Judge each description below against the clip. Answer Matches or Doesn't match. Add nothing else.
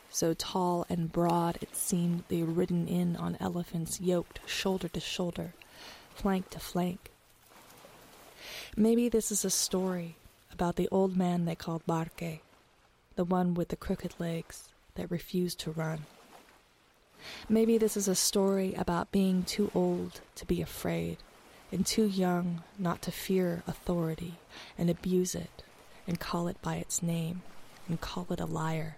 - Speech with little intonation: Matches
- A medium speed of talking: Matches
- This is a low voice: Doesn't match